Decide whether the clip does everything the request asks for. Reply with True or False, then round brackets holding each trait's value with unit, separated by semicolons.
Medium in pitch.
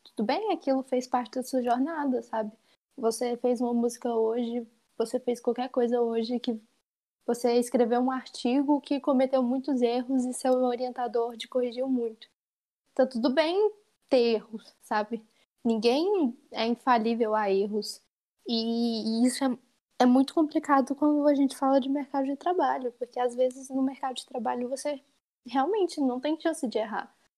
False (250 Hz)